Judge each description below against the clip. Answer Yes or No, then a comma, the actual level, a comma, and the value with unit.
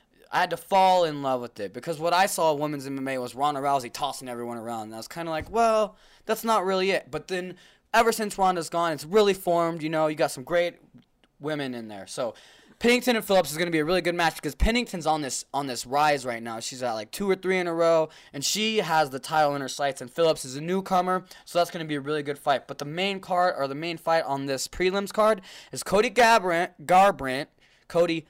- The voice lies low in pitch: No, medium, 165 Hz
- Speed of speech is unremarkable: No, fast, 250 wpm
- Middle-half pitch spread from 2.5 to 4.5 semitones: No, average, 5.1 semitones